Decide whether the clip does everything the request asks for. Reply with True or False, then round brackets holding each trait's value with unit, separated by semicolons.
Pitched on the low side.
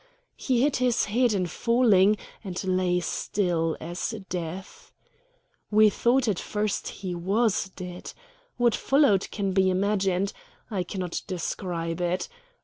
False (190 Hz)